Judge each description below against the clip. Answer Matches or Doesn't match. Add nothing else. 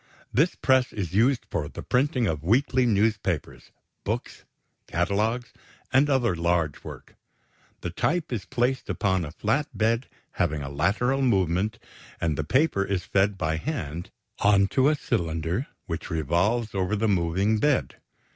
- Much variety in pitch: Matches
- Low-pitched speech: Matches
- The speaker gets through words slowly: Doesn't match